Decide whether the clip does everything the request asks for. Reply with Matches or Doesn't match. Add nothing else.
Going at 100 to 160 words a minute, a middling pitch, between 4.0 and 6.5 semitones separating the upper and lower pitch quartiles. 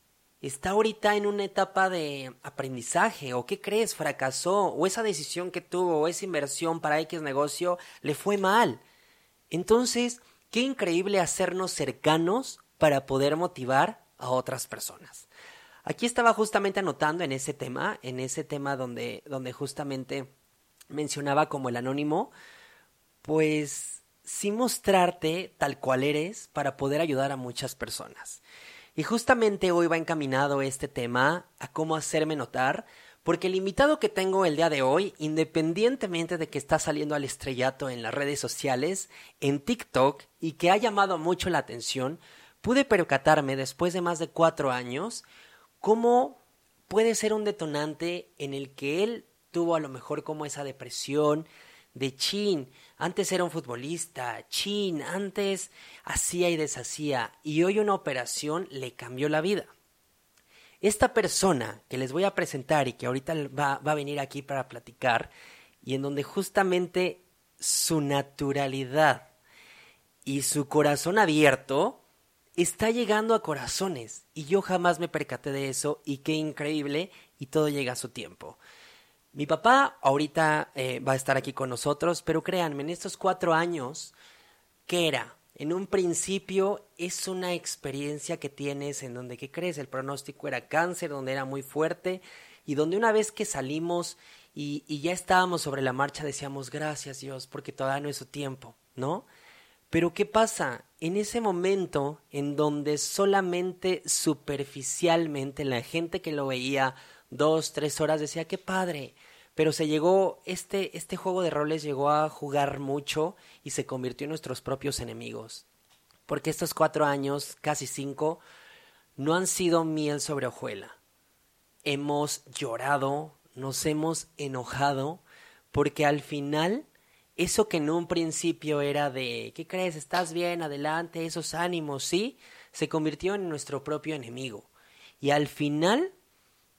Matches